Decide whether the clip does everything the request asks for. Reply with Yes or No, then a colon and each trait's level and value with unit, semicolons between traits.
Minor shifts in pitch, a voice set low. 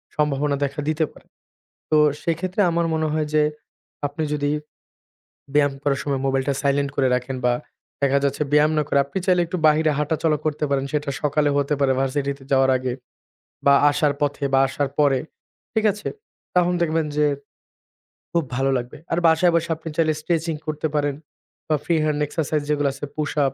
No: narrow, 2.2 semitones; medium, 150 Hz